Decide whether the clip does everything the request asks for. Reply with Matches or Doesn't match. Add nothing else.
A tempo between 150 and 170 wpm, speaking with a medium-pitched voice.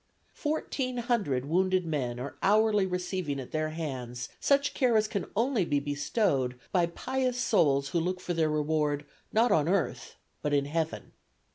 Matches